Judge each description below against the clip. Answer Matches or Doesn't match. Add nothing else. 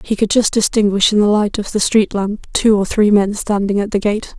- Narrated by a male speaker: Doesn't match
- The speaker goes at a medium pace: Doesn't match